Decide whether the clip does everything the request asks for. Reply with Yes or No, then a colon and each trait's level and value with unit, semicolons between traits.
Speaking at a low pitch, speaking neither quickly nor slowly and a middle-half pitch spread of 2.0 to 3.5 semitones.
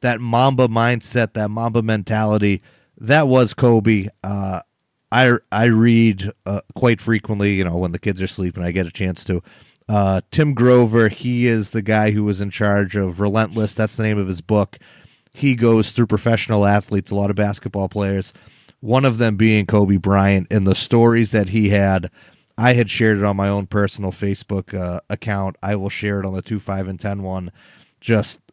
Yes: low, 105 Hz; average, 195 wpm; average, 2.8 semitones